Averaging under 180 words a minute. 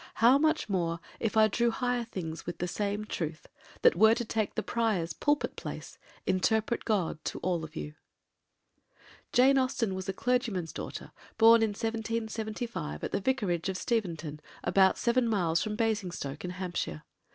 Yes: average, 165 wpm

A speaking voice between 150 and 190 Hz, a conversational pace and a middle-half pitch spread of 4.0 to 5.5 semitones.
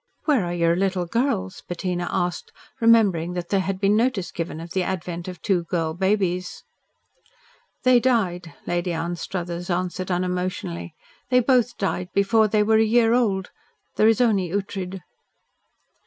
No: medium, 185 Hz; average, 150 wpm; average, 3.5 semitones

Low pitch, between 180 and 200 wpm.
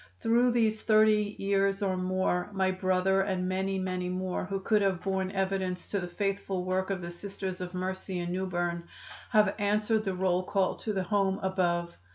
No: high, 190 Hz; average, 190 wpm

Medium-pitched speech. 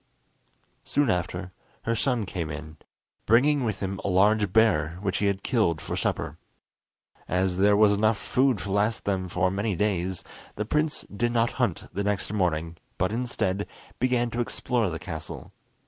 No: low, 100 Hz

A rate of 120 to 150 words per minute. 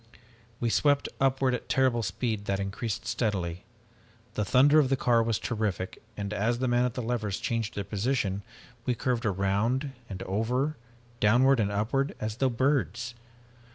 No: average, 160 wpm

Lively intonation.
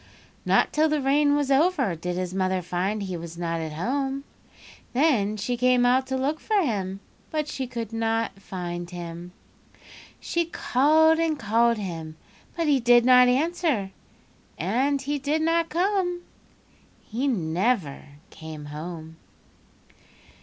Yes: wide, 8.1 semitones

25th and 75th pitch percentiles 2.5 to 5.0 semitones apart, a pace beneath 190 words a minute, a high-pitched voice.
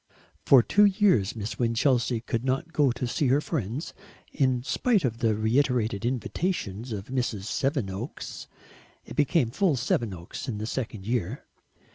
No: average, 3.9 semitones; average, 145 wpm; low, 125 Hz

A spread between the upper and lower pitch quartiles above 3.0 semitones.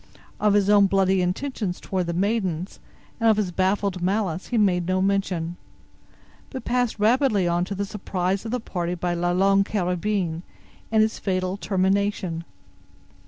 No: narrow, 2.6 semitones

